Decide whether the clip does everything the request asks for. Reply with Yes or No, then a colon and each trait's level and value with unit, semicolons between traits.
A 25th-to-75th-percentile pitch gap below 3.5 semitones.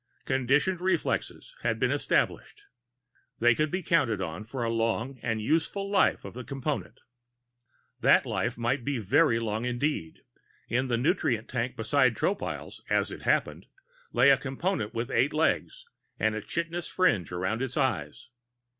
No: average, 5.2 semitones